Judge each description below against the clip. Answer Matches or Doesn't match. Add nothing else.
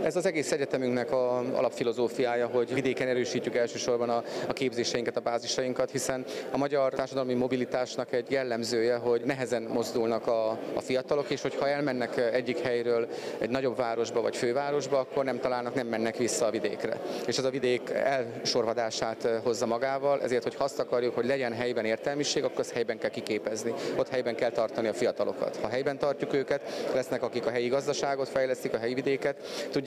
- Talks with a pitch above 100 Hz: Matches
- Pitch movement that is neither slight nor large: Doesn't match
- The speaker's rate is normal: Doesn't match